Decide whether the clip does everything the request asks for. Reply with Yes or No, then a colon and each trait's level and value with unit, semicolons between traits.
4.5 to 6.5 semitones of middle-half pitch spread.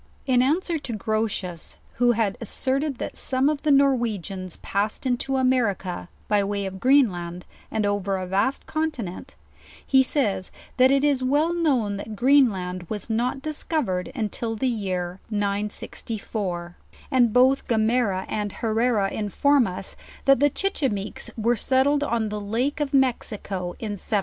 Yes: average, 5.1 semitones